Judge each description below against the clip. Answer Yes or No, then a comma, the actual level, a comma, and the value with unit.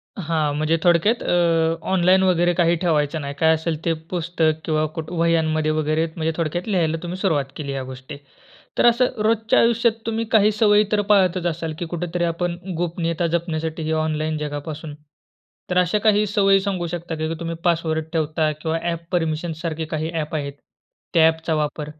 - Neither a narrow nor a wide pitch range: No, narrow, 2.1 semitones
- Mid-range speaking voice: Yes, medium, 165 Hz